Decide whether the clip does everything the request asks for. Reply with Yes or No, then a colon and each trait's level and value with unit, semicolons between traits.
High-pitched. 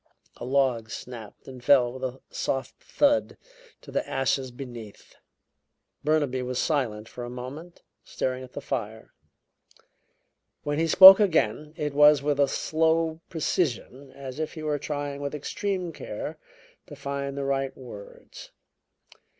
No: medium, 140 Hz